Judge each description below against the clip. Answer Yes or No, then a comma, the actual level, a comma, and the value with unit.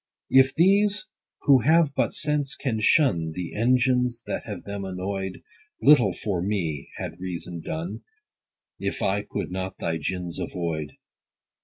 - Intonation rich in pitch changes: Yes, wide, 6.8 semitones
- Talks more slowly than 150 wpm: Yes, average, 140 wpm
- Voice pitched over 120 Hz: No, low, 100 Hz